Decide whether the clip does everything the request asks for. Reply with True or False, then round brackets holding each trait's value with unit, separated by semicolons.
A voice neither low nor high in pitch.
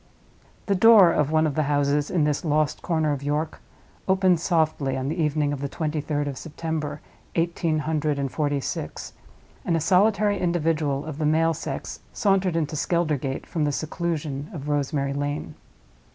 True (155 Hz)